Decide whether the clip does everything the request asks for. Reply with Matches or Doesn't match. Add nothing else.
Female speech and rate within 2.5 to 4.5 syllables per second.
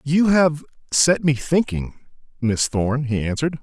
Doesn't match